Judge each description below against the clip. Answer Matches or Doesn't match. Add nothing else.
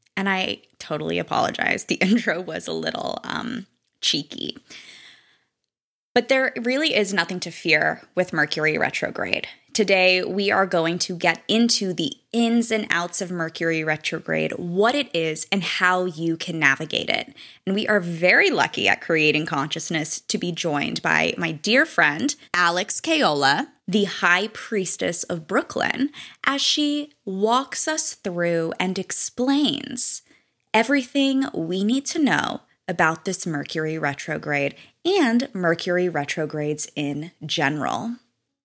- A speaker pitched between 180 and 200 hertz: Matches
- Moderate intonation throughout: Doesn't match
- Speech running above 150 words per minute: Doesn't match